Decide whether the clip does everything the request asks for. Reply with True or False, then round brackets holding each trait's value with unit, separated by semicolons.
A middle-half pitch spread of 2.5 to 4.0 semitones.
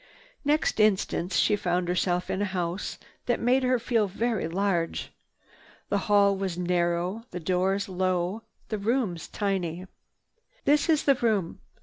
True (3.7 semitones)